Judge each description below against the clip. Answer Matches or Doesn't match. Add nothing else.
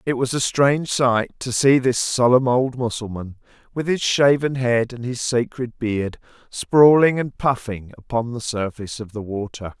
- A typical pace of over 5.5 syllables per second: Doesn't match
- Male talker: Matches